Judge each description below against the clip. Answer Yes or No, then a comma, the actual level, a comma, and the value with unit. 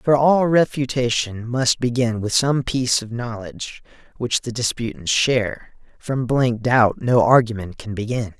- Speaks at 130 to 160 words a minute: Yes, average, 150 wpm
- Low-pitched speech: Yes, low, 120 Hz